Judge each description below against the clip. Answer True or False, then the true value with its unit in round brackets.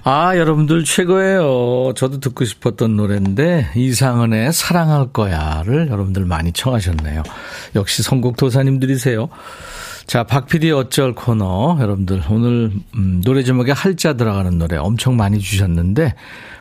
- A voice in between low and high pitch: False (125 Hz)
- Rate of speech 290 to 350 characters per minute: True (315 characters per minute)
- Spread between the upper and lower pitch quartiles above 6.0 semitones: False (5.6 semitones)